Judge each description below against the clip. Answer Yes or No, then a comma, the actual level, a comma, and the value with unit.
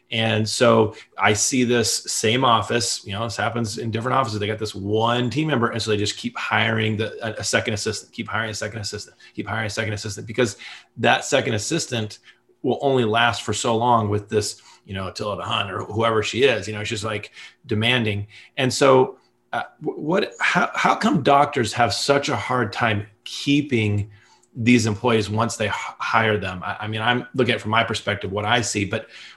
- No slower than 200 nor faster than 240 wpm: Yes, fast, 205 wpm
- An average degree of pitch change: No, narrow, 2.2 semitones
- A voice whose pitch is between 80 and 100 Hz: No, low, 110 Hz